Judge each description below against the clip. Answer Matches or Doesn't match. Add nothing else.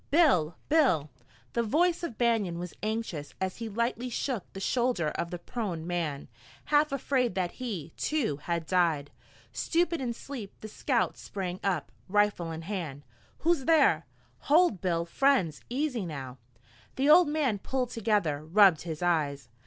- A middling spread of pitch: Doesn't match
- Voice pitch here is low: Doesn't match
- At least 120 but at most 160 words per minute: Matches